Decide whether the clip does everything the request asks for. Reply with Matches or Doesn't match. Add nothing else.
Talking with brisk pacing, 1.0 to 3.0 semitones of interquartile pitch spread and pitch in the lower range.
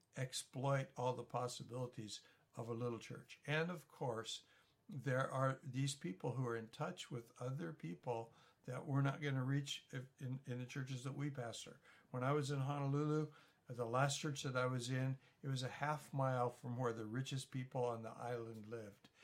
Doesn't match